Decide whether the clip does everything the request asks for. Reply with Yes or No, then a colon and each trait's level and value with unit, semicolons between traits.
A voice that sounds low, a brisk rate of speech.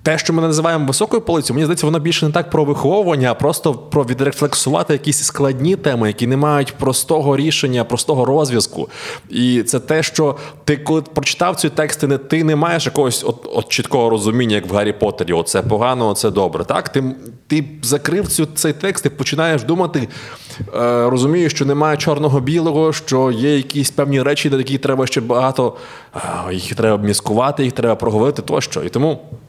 No: medium, 145 Hz; fast, 175 wpm